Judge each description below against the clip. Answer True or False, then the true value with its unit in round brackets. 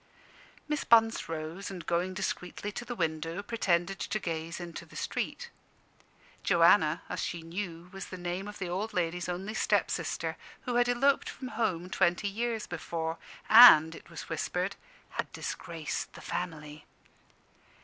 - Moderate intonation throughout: True (4.2 semitones)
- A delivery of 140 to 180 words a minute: True (150 wpm)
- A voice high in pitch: False (180 Hz)